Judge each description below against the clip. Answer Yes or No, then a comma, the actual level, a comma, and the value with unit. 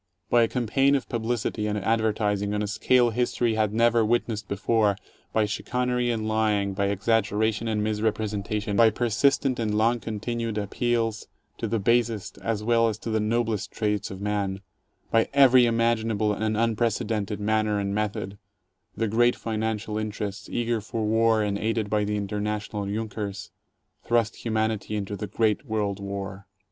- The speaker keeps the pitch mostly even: Yes, narrow, 1.8 semitones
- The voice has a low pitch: Yes, low, 110 Hz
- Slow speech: No, average, 155 wpm